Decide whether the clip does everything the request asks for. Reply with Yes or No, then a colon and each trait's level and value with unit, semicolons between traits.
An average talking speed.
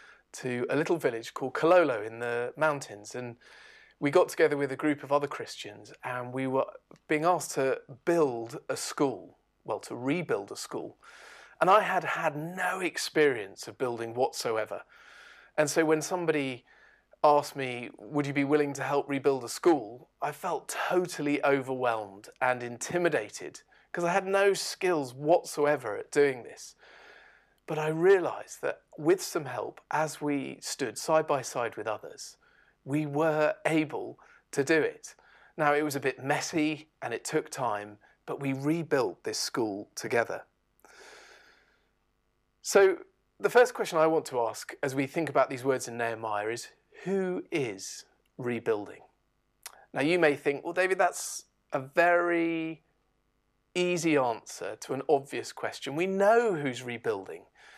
Yes: average, 155 wpm